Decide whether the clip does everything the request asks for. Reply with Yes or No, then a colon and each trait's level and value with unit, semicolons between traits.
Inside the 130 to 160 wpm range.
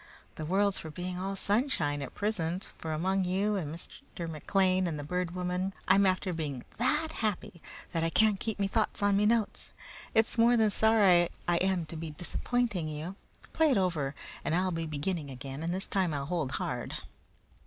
No: average, 190 wpm